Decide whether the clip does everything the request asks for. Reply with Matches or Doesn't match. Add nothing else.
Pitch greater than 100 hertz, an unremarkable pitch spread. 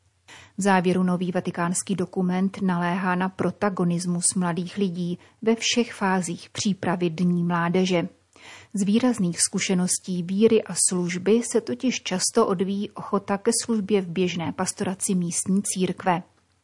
Doesn't match